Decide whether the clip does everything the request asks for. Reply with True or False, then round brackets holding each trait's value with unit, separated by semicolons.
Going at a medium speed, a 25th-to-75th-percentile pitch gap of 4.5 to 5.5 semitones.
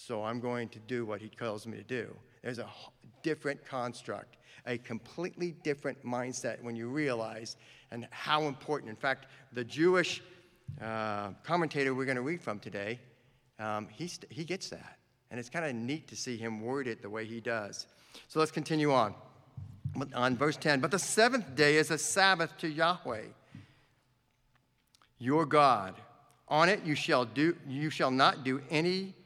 True (175 wpm; 4.9 semitones)